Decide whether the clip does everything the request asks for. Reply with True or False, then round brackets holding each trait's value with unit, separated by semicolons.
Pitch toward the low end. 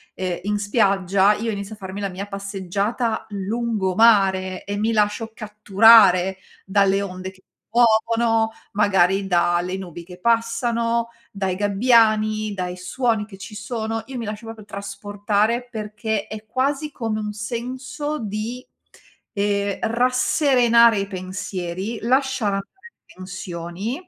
False (210 Hz)